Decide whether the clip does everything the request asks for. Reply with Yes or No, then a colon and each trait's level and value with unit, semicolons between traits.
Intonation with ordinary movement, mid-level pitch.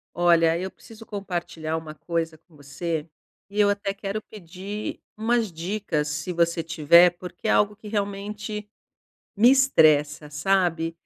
Yes: average, 4.1 semitones; medium, 180 Hz